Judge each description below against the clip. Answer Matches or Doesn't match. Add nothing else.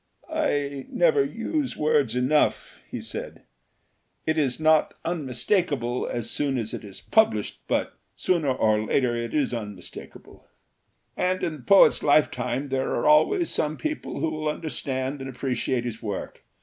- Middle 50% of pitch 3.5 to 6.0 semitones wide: Matches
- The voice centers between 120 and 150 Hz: Matches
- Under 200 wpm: Matches